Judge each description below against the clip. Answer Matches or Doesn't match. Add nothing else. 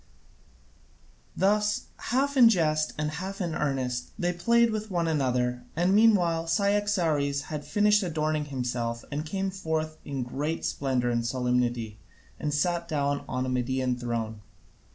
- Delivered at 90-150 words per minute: Matches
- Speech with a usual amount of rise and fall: Doesn't match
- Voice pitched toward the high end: Doesn't match